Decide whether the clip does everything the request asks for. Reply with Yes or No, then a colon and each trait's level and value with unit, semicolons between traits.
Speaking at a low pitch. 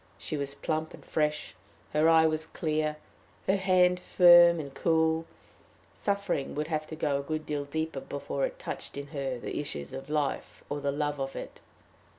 No: medium, 155 Hz